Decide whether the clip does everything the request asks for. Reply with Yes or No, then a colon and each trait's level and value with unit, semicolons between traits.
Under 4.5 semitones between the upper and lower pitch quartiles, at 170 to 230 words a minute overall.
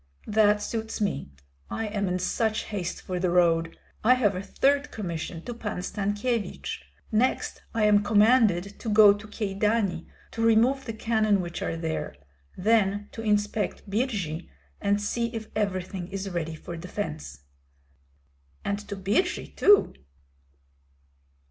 No: average, 3.4 semitones; average, 140 wpm